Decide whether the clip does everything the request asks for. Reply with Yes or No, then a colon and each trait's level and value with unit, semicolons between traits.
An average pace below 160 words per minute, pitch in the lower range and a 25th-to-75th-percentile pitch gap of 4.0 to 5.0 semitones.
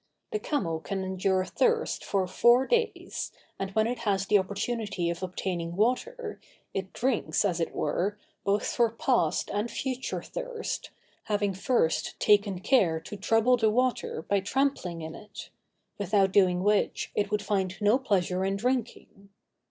No: average, 150 wpm; high, 205 Hz; average, 4.3 semitones